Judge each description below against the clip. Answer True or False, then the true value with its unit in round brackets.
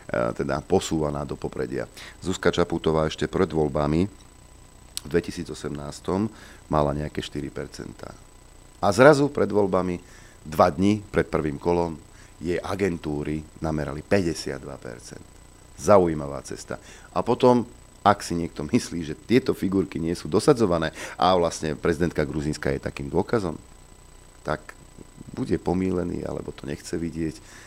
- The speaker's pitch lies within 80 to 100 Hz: True (85 Hz)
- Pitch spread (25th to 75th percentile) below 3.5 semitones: False (4.4 semitones)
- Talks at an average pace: True (120 wpm)